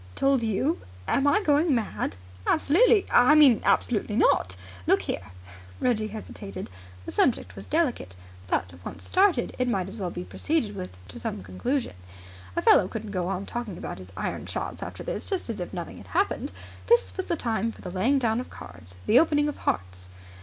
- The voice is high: Yes, high, 225 Hz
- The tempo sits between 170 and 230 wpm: Yes, average, 190 wpm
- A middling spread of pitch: No, wide, 8.0 semitones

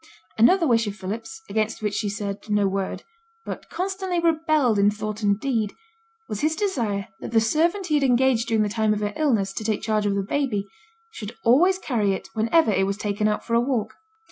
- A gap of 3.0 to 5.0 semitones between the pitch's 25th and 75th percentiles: No, wide, 5.6 semitones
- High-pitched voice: Yes, high, 220 Hz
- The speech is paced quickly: Yes, fast, 210 wpm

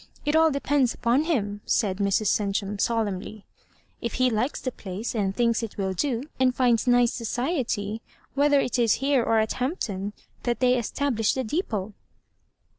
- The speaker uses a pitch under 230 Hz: No, high, 235 Hz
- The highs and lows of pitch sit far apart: No, average, 3.9 semitones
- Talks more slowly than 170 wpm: No, average, 175 wpm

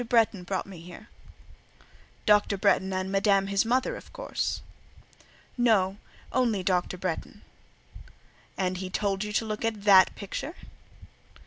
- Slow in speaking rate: Yes, slow, 130 wpm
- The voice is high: Yes, high, 200 Hz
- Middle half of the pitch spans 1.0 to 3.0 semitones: Yes, narrow, 2.4 semitones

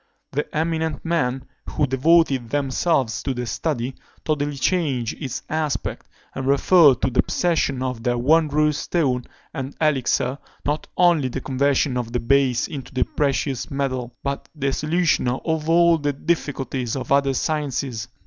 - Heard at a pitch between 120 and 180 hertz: Yes, medium, 140 Hz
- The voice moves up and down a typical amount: Yes, average, 3.2 semitones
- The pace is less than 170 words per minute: Yes, average, 150 wpm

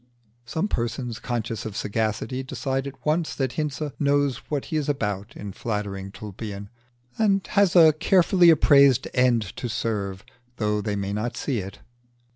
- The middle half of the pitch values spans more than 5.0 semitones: Yes, wide, 5.5 semitones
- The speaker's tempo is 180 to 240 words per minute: No, average, 155 wpm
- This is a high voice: No, low, 120 Hz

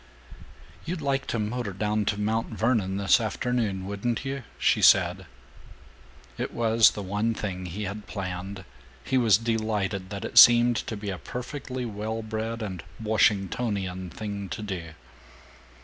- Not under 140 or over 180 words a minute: Yes, average, 150 wpm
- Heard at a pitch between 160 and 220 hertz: No, low, 105 Hz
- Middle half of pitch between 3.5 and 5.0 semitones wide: No, average, 2.8 semitones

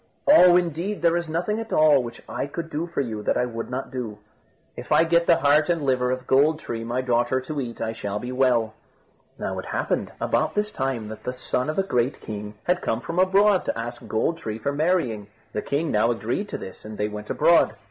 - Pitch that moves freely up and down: Yes, wide, 6.4 semitones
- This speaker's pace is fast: Yes, fast, 235 wpm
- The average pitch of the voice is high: No, low, 130 Hz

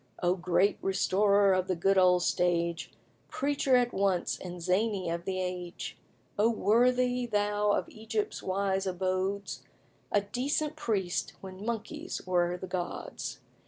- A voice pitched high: Yes, high, 195 Hz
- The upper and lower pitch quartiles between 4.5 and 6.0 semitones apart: No, average, 3.4 semitones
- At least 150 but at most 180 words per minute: No, slow, 135 wpm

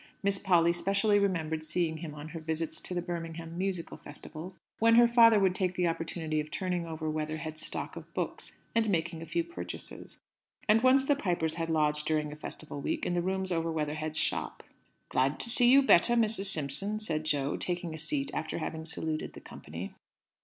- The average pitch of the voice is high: No, medium, 165 Hz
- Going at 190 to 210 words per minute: Yes, average, 195 wpm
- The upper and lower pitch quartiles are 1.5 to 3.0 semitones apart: No, average, 3.8 semitones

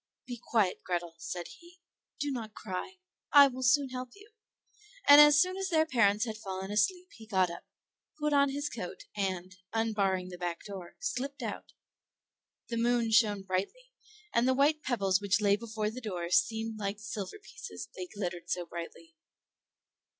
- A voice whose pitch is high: Yes, high, 220 Hz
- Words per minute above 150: Yes, average, 170 wpm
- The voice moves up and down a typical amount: No, wide, 6.6 semitones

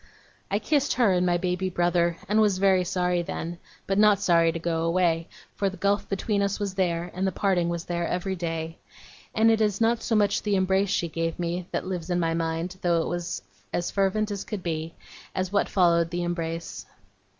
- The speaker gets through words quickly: Yes, fast, 210 wpm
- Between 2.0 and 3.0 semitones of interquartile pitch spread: Yes, average, 2.7 semitones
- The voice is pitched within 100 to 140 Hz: No, medium, 180 Hz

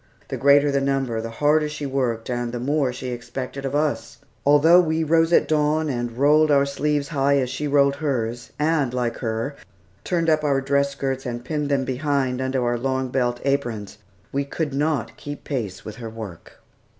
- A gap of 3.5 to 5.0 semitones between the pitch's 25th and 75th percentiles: No, average, 3.1 semitones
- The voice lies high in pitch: No, medium, 140 Hz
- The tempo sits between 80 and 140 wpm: No, average, 190 wpm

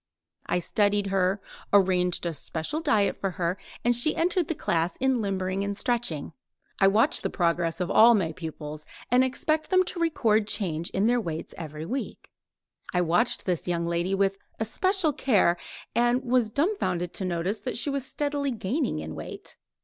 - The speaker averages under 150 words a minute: No, average, 175 wpm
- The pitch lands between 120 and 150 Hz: No, high, 200 Hz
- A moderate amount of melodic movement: No, wide, 6.4 semitones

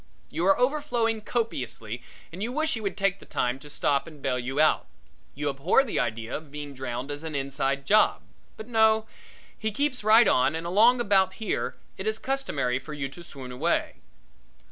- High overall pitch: No, medium, 170 Hz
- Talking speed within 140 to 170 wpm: No, average, 190 wpm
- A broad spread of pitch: Yes, wide, 8.2 semitones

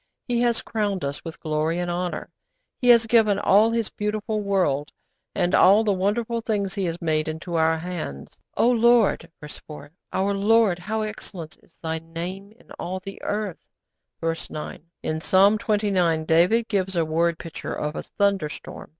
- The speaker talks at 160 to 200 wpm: Yes, average, 170 wpm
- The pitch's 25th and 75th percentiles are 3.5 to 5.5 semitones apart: Yes, average, 4.5 semitones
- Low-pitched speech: No, high, 190 Hz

